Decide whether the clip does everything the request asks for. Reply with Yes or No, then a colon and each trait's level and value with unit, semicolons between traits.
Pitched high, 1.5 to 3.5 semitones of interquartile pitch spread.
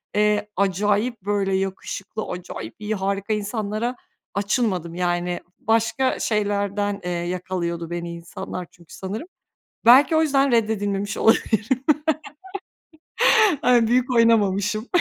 Yes: high, 205 Hz; average, 3.1 semitones